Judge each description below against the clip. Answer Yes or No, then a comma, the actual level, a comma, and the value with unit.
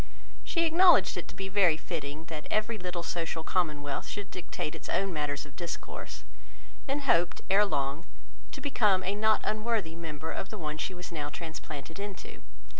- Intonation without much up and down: No, average, 4.9 semitones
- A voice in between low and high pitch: Yes, medium, 175 Hz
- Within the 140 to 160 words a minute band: No, average, 175 wpm